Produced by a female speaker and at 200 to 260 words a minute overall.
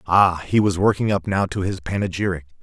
No: male; fast, 205 wpm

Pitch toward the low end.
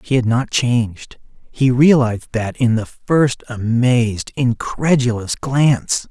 Yes: low, 125 Hz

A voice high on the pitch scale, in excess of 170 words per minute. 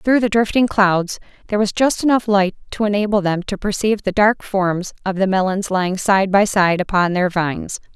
Yes: high, 200 Hz; fast, 205 wpm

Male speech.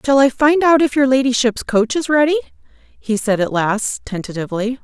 No: female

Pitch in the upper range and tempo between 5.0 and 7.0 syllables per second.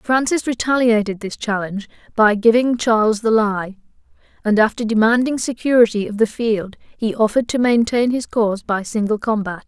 Yes: high, 225 Hz; 5.3 syllables/s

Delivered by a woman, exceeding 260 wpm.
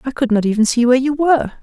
Yes: female; fast, 295 wpm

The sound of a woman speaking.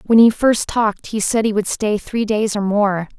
Yes: female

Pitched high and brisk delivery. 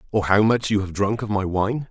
No: low, 105 Hz; fast, 285 wpm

